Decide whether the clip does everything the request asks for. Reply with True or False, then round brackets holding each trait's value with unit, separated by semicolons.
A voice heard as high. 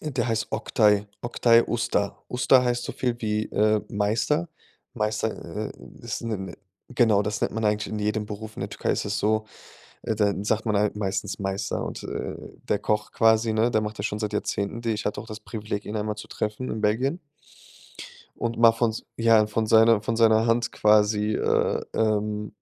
False (110 Hz)